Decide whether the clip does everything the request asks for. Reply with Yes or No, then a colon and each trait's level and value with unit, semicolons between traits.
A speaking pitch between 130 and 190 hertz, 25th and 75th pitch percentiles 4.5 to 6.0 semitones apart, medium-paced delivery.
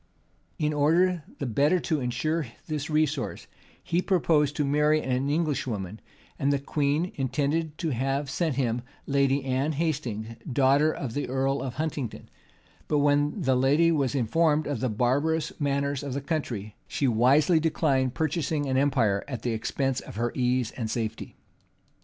No: medium, 140 Hz; average, 3.1 semitones; average, 160 wpm